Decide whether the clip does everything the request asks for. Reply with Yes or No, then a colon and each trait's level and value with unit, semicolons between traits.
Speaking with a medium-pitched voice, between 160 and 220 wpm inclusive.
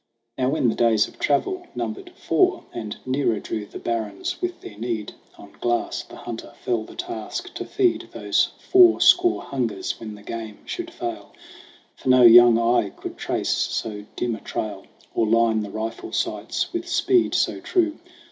No: low, 120 Hz; average, 175 wpm